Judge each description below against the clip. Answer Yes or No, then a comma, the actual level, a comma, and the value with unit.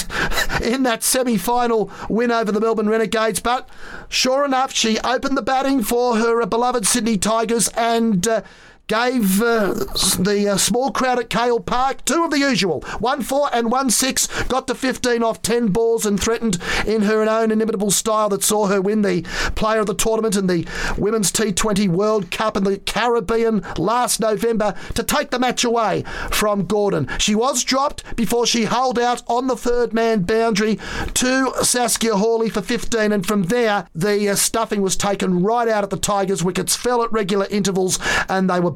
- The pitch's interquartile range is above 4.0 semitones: No, average, 2.7 semitones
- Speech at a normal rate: Yes, average, 185 wpm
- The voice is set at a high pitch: Yes, high, 225 Hz